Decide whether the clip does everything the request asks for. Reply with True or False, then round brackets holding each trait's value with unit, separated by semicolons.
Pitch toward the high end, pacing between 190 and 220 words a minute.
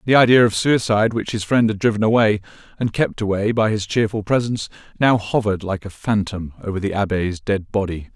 False (105 Hz; 200 wpm)